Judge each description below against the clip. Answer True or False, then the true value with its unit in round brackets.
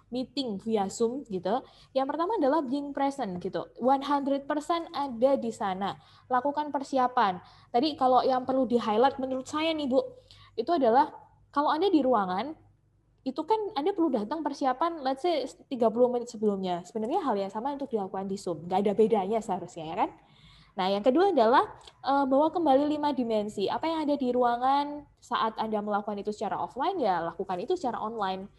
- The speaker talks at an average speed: False (170 wpm)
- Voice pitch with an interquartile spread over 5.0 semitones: True (5.6 semitones)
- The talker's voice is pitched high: True (260 Hz)